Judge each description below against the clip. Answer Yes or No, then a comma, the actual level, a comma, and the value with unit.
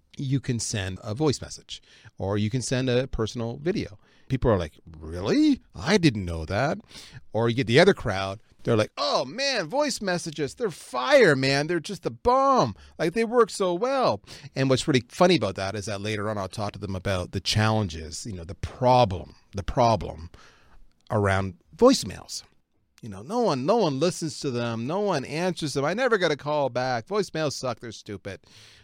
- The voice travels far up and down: Yes, wide, 7.7 semitones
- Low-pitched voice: Yes, low, 120 Hz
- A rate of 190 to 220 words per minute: Yes, average, 195 wpm